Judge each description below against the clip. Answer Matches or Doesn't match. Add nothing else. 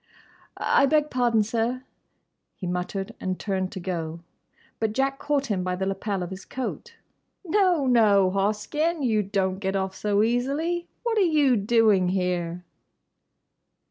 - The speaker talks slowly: Doesn't match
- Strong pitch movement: Matches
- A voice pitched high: Matches